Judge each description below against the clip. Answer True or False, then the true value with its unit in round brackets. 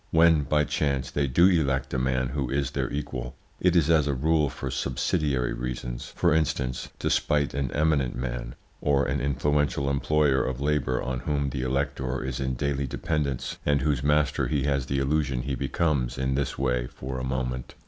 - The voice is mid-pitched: False (70 Hz)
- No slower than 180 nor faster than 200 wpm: True (190 wpm)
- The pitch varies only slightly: True (2.3 semitones)